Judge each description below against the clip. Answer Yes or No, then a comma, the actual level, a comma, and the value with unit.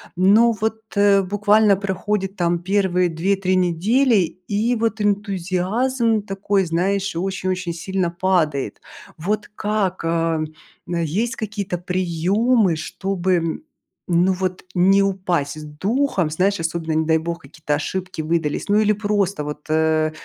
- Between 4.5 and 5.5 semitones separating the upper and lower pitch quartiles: No, average, 3.3 semitones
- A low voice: No, medium, 185 Hz